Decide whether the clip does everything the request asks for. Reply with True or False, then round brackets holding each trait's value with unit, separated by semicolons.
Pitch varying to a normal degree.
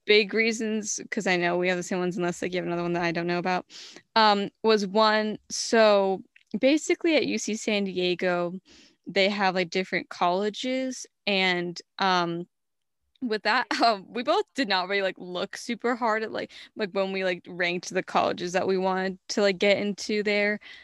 True (3.3 semitones)